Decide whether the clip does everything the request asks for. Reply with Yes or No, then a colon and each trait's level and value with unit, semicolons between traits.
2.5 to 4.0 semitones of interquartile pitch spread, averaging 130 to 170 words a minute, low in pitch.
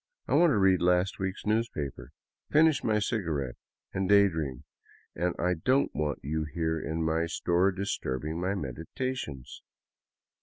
No: average, 4.4 semitones; average, 150 wpm; very low, 90 Hz